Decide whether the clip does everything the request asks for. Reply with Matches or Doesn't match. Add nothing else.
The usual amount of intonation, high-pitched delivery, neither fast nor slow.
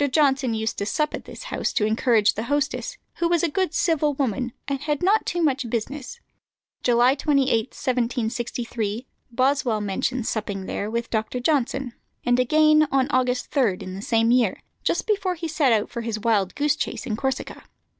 Matches